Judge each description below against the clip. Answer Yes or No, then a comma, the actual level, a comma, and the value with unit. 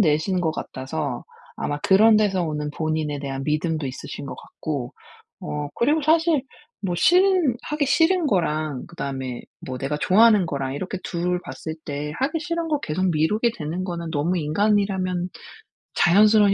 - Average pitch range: No, wide, 6.2 semitones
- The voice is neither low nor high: Yes, medium, 175 Hz